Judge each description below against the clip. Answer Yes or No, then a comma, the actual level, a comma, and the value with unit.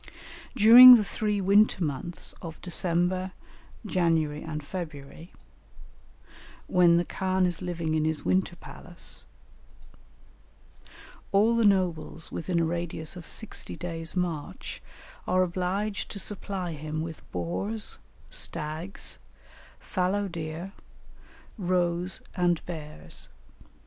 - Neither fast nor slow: No, slow, 105 wpm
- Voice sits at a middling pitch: Yes, medium, 175 Hz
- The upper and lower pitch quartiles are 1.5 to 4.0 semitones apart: Yes, average, 2.8 semitones